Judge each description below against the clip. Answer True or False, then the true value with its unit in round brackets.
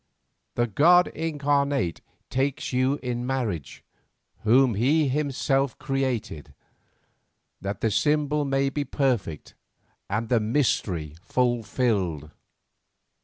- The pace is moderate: False (95 wpm)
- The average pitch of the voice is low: True (130 Hz)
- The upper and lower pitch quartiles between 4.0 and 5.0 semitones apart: True (4.4 semitones)